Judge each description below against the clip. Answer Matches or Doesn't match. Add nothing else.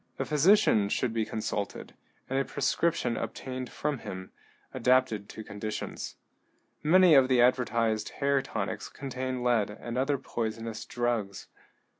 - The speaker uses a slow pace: Matches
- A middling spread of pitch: Matches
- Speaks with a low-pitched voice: Matches